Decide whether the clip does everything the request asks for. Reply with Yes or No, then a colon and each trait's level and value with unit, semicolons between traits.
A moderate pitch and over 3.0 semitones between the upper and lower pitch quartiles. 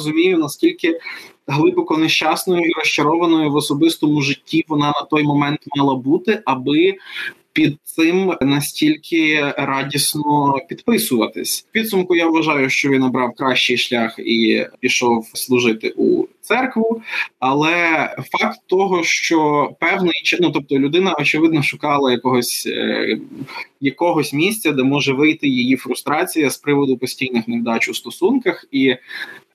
Yes: medium, 150 Hz; average, 4.9 semitones